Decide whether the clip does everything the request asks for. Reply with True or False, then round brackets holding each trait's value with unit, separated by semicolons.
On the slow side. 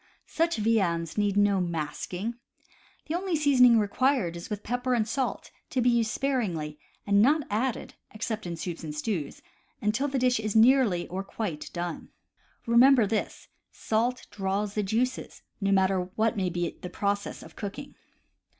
False (160 wpm)